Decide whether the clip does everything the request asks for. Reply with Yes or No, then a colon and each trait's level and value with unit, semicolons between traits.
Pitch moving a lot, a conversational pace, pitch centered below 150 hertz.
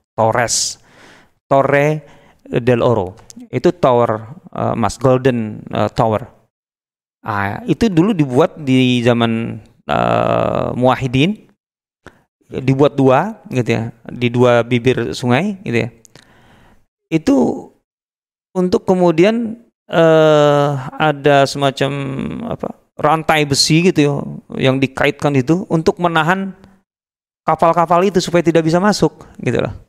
Yes: wide, 5.7 semitones; average, 105 wpm; medium, 140 Hz